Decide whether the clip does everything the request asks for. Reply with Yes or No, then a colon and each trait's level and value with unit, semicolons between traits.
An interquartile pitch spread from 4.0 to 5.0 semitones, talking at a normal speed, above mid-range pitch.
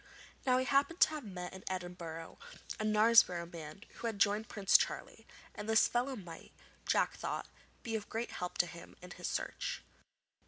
Yes: average, 4.6 semitones; average, 180 wpm; high, 205 Hz